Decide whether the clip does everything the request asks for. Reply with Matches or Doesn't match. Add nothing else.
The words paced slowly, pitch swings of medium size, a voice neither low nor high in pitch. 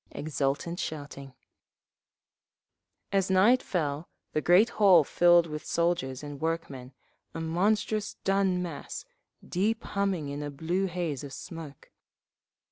Matches